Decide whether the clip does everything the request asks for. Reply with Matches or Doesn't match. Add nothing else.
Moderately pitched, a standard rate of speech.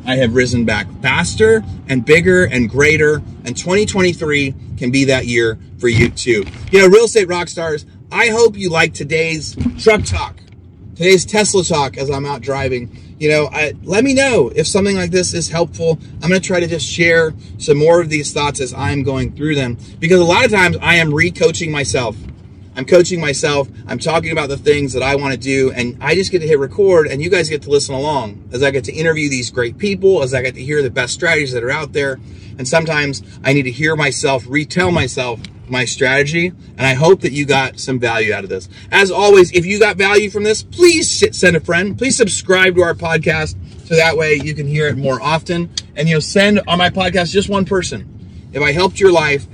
Doesn't match